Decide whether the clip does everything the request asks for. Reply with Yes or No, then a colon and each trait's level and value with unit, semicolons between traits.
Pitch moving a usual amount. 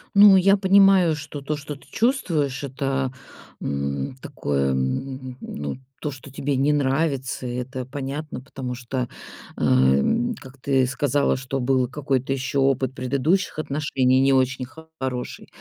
No: narrow, 2.3 semitones